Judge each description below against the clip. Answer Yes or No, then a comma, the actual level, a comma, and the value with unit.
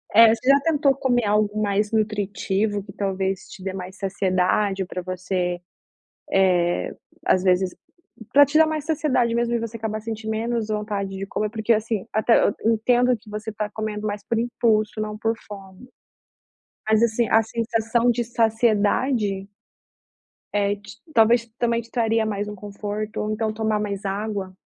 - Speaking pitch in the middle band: No, high, 215 Hz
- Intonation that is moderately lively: No, narrow, 2.2 semitones